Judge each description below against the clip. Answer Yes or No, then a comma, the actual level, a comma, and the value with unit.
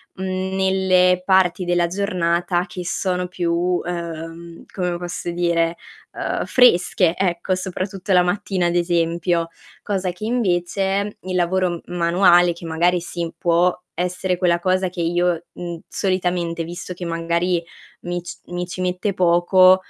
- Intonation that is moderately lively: No, narrow, 1.3 semitones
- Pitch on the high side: No, medium, 180 Hz